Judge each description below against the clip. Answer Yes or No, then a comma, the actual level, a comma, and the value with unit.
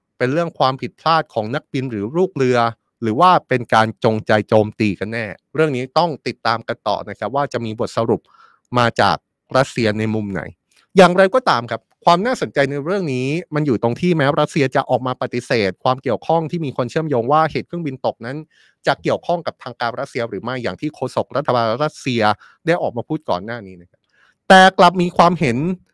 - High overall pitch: No, low, 130 Hz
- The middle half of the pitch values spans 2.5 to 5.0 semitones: No, wide, 5.5 semitones